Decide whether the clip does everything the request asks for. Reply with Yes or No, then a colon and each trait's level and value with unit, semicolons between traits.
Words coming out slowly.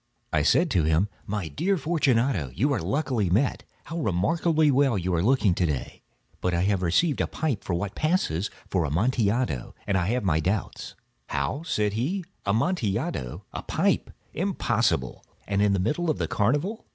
No: average, 175 wpm